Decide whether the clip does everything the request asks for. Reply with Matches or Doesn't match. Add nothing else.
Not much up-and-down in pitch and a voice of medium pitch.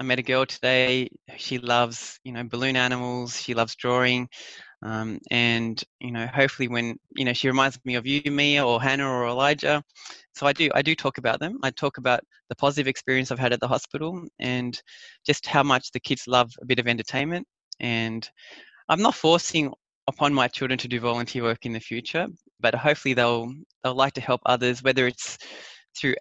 Doesn't match